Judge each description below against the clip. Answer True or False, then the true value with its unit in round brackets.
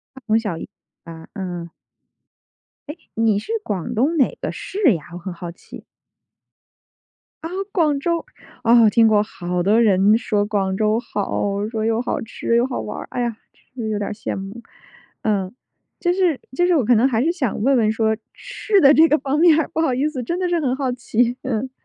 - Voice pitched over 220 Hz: True (230 Hz)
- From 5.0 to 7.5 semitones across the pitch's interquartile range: True (5.3 semitones)